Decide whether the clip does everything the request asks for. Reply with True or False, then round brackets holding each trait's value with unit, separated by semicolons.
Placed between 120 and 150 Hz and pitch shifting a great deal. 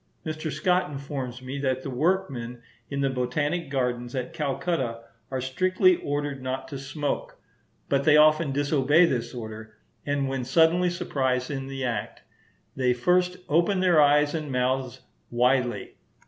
False (140 Hz; 3.3 semitones)